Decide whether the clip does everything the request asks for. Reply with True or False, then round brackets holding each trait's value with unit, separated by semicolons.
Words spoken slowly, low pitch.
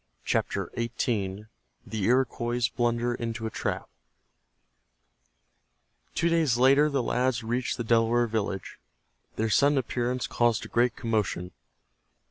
True (110 wpm; 120 Hz)